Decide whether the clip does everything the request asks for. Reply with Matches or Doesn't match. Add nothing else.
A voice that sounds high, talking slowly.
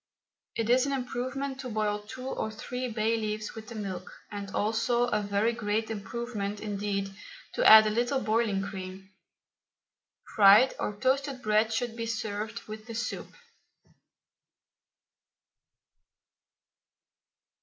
Matches